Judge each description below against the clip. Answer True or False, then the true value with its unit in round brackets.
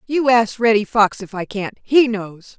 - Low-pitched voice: False (220 Hz)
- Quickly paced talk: True (210 wpm)